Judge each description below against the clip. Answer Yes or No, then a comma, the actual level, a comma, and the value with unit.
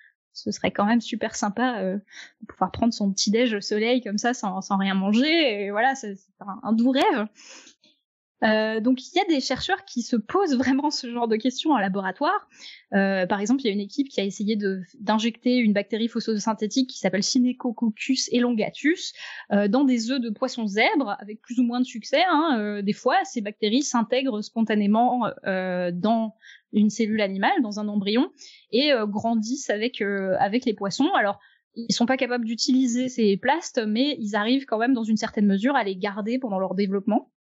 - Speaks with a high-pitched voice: Yes, high, 230 Hz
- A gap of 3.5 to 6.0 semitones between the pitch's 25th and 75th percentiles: Yes, average, 3.8 semitones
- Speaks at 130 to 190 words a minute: No, average, 205 wpm